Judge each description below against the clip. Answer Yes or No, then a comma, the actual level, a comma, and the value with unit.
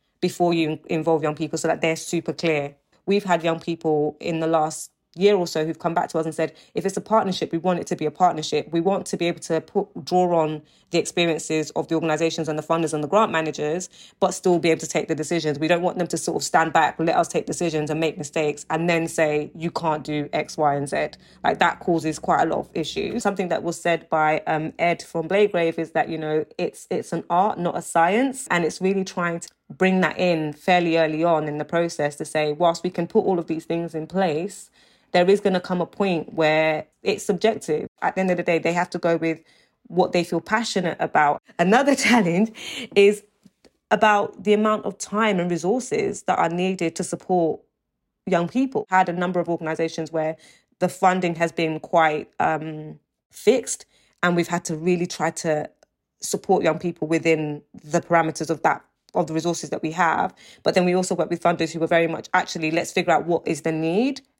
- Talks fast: Yes, fast, 225 wpm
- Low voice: No, medium, 170 Hz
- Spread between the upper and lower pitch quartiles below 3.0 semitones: Yes, narrow, 2.4 semitones